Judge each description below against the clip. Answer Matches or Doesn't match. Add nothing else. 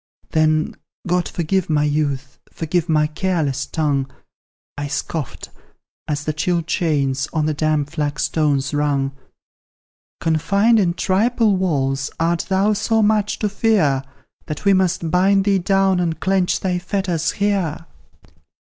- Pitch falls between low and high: Matches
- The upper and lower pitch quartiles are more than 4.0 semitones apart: Matches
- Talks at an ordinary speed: Doesn't match